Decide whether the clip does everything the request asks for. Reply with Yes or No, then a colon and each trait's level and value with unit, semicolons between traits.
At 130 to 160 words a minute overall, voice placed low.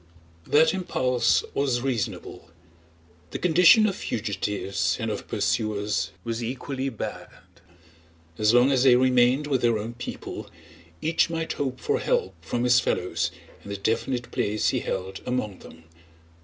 Yes: average, 140 wpm; low, 120 Hz